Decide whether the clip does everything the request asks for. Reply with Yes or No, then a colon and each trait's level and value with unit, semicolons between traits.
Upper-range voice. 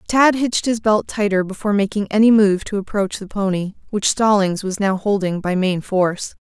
Yes: high, 200 Hz